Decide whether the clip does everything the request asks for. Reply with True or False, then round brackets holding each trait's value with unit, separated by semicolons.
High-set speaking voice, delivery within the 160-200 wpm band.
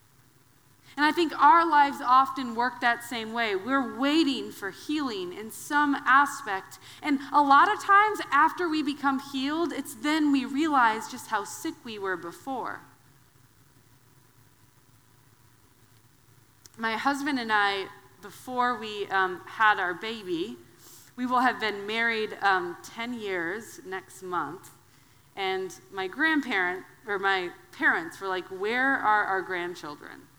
False (220 Hz; 135 wpm)